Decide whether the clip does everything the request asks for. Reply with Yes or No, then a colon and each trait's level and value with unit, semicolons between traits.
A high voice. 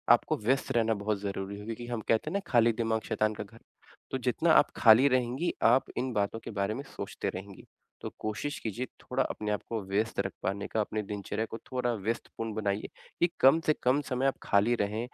No: low, 110 Hz